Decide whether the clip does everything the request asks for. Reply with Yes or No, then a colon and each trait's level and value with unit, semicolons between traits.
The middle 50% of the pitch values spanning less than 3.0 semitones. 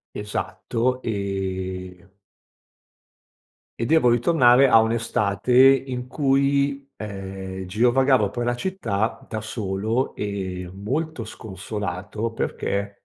No: average, 4.5 semitones